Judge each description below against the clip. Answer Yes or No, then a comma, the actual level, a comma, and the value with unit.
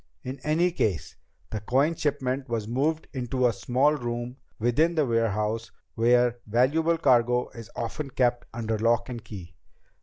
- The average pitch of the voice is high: No, low, 120 Hz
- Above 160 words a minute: No, average, 150 wpm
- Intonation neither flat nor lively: Yes, average, 3.1 semitones